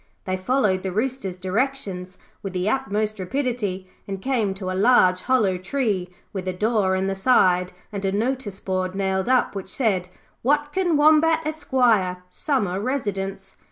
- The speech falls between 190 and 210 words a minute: No, average, 155 wpm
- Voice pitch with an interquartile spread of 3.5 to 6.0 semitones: Yes, wide, 5.5 semitones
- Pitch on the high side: Yes, high, 200 Hz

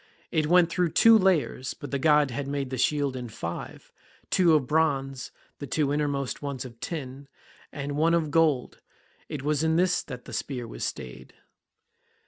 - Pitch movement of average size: Yes, average, 3.4 semitones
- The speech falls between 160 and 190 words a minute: Yes, average, 175 wpm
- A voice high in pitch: No, medium, 145 Hz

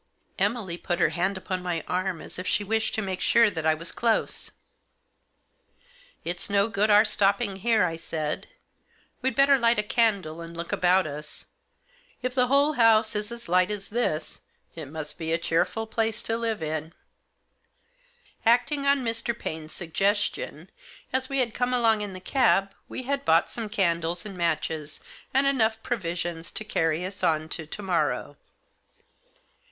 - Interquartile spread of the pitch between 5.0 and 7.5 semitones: Yes, wide, 5.4 semitones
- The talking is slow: No, average, 170 wpm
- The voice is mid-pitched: No, high, 200 Hz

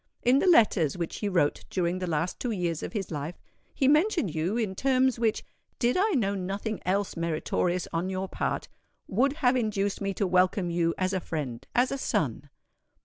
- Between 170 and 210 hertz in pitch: Yes, high, 190 Hz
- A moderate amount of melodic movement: No, wide, 5.7 semitones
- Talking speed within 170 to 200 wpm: Yes, average, 190 wpm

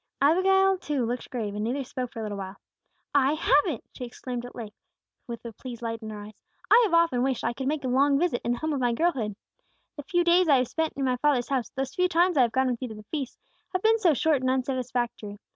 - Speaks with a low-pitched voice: No, very high, 260 Hz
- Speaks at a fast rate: Yes, fast, 260 wpm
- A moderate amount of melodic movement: Yes, average, 4.6 semitones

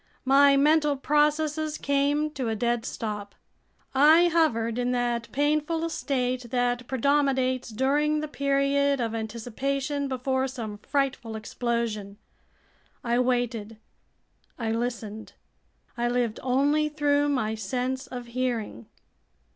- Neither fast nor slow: No, slow, 115 wpm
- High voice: Yes, very high, 255 Hz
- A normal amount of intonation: Yes, average, 3.4 semitones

